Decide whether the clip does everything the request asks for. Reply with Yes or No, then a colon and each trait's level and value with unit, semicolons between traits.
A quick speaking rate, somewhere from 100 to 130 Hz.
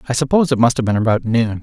Yes: fast, 295 wpm; low, 120 Hz